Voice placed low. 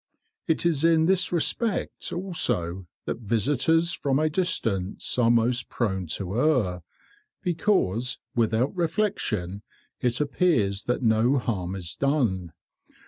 Yes: low, 125 Hz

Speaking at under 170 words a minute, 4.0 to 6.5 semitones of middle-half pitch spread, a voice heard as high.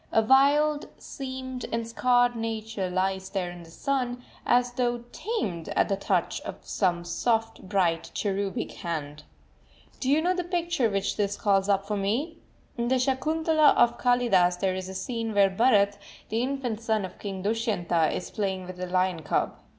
No: average, 175 wpm; average, 4.9 semitones; high, 220 Hz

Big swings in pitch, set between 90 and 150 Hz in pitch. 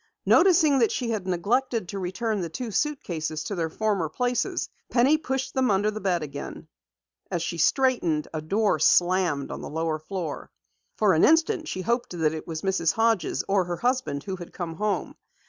No: wide, 6.6 semitones; high, 195 Hz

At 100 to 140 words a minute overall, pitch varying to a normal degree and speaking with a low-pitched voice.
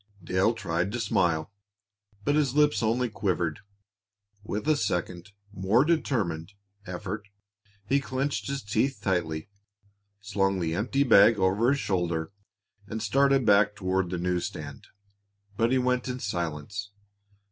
No: slow, 135 wpm; wide, 5.7 semitones; low, 105 Hz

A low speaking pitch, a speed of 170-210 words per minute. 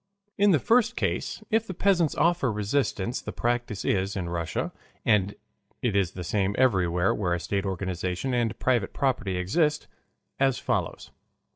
No: low, 105 Hz; average, 155 wpm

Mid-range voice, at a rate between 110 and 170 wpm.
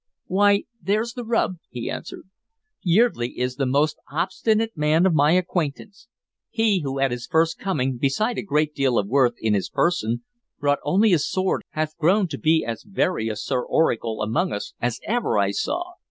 No: medium, 155 Hz; average, 185 wpm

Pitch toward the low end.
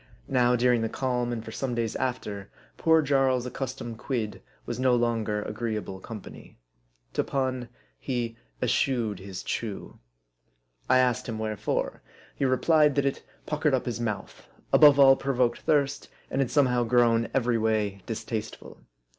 Yes: low, 120 Hz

